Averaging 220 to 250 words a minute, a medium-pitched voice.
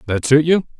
Yes: fast, 225 wpm; medium, 145 Hz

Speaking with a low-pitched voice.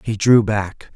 Yes: low, 105 Hz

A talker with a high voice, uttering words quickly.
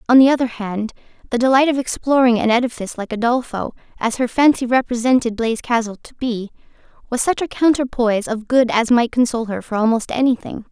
No: high, 240 Hz; average, 185 wpm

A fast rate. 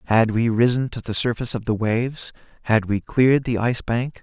Yes: fast, 215 wpm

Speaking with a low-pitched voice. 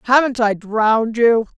No: high, 230 Hz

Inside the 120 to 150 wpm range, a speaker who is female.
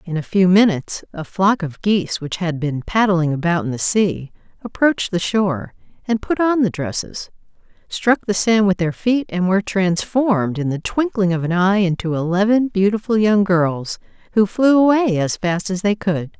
No: average, 190 wpm; female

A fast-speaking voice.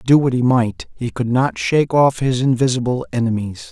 No: average, 195 wpm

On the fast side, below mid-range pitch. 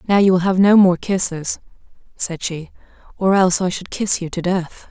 No: fast, 210 wpm; medium, 185 Hz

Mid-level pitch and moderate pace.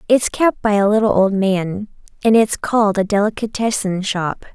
No: high, 205 Hz; average, 170 wpm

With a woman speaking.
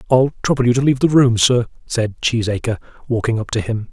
No: male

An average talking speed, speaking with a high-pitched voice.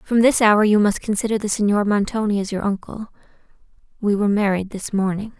Yes: average, 180 wpm; high, 205 Hz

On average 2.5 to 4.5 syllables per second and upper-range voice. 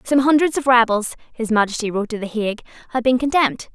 No: 6.8 syllables/s; high, 240 Hz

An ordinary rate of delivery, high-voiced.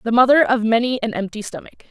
No: fast, 220 wpm; high, 230 Hz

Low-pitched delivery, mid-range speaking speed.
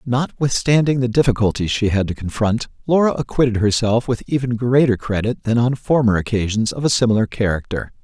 Yes: low, 115 Hz; average, 165 wpm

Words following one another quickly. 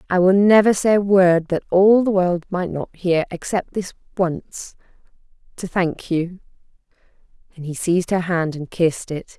No: average, 160 wpm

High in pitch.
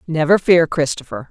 No: medium, 165 Hz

